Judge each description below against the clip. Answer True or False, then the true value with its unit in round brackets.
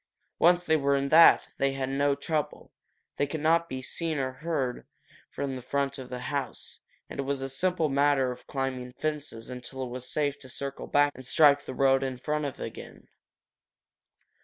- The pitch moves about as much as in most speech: False (2.2 semitones)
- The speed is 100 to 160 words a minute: False (185 wpm)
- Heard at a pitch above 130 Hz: True (140 Hz)